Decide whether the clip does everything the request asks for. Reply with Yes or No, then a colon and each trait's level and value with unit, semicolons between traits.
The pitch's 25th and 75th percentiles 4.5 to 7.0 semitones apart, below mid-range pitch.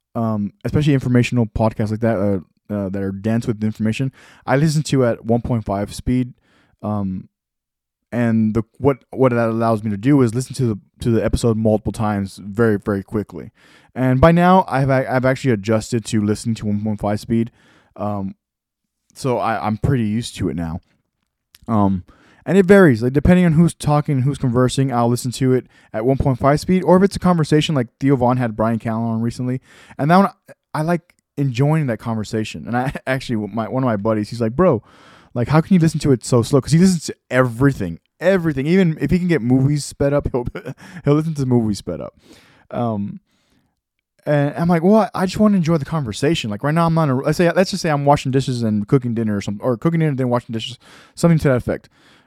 Yes: average, 4.8 semitones; low, 125 Hz